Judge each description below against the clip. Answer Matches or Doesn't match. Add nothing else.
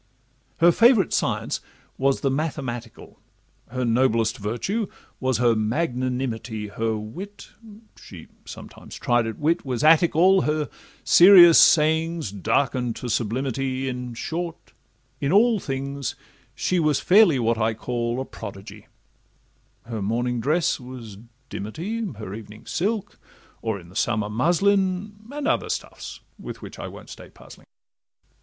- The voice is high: Doesn't match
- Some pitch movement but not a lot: Doesn't match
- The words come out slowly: Matches